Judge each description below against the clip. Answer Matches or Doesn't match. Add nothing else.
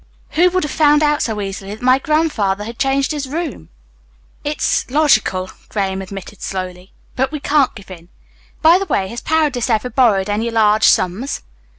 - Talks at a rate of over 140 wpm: Matches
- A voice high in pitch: Matches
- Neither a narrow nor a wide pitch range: Doesn't match